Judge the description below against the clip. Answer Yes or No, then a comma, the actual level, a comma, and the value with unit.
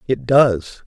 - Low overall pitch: Yes, low, 120 Hz